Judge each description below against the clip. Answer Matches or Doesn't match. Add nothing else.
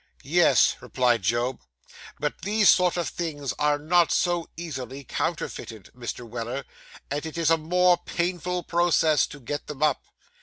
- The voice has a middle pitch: Matches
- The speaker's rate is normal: Matches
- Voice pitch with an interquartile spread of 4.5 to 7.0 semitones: Matches